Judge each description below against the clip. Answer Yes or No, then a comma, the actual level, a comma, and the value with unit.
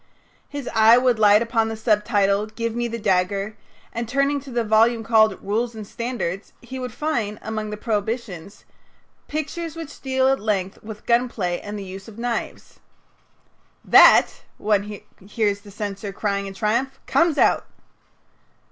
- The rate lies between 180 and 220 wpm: No, average, 155 wpm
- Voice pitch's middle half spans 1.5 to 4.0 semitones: Yes, average, 2.9 semitones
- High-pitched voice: Yes, high, 220 Hz